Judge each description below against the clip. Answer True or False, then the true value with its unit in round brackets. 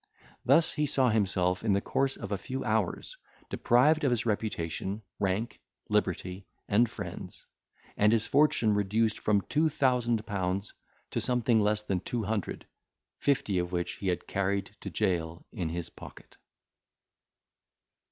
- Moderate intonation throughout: True (4.0 semitones)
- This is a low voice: True (105 Hz)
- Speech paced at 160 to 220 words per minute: False (145 wpm)